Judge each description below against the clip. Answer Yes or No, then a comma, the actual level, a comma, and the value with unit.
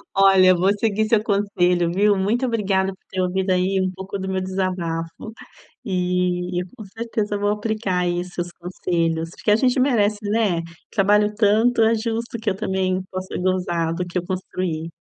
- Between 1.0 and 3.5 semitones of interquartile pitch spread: Yes, narrow, 2.6 semitones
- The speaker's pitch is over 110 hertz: Yes, high, 190 Hz